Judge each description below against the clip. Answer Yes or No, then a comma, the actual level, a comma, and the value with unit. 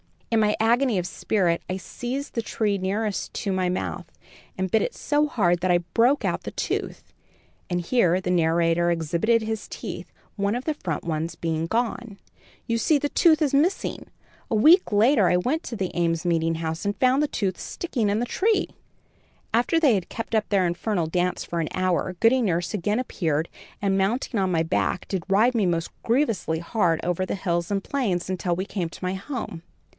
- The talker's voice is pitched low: No, high, 195 Hz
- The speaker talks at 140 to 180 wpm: No, average, 200 wpm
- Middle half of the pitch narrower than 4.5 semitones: No, average, 5.1 semitones